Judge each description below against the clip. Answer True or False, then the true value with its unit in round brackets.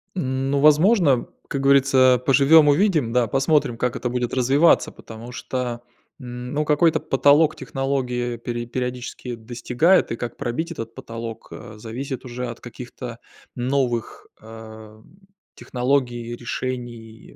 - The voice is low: True (125 Hz)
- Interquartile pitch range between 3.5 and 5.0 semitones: False (2.7 semitones)